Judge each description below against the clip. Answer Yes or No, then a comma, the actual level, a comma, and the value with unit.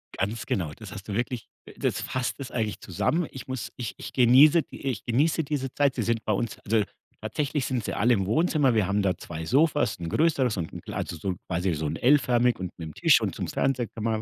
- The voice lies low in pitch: Yes, low, 115 Hz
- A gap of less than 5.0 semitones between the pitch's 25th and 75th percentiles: No, wide, 5.4 semitones